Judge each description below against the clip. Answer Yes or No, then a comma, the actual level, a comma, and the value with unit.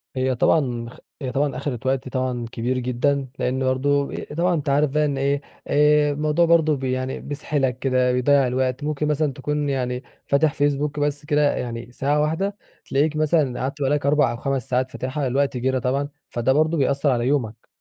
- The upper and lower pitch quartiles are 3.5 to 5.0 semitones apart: No, narrow, 2.4 semitones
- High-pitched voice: No, medium, 140 Hz